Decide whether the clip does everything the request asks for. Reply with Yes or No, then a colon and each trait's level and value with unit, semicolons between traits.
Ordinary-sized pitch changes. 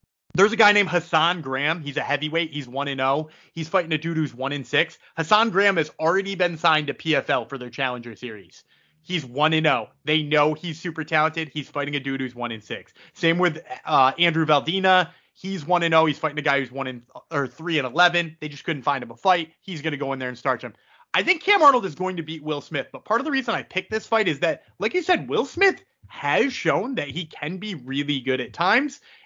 Yes: average, 4.3 semitones